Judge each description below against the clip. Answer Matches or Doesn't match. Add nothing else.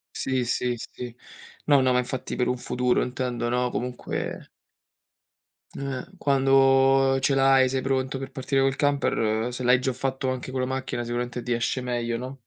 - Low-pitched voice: Matches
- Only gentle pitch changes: Matches